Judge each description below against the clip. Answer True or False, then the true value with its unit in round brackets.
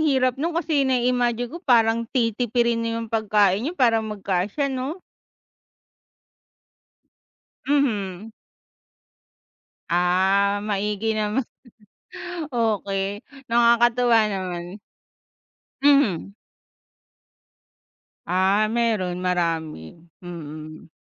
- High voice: True (220 Hz)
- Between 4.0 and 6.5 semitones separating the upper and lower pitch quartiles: True (4.3 semitones)